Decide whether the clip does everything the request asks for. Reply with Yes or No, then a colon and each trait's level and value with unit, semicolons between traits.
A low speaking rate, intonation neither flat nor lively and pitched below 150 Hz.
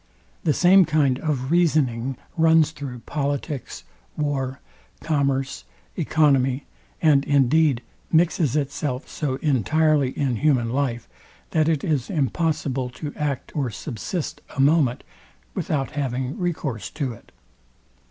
Yes: slow, 115 wpm; average, 3.2 semitones; medium, 140 Hz